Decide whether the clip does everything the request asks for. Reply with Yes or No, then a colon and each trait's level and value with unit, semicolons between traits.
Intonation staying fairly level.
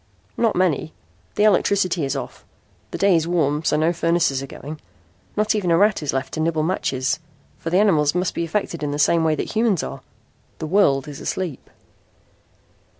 No: average, 4.0 semitones